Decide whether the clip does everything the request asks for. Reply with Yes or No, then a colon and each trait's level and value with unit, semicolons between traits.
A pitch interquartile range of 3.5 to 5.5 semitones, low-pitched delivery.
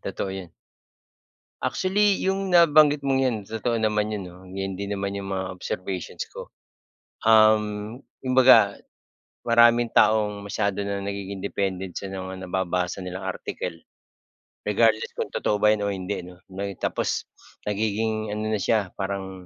No: average, 2.7 semitones; low, 100 Hz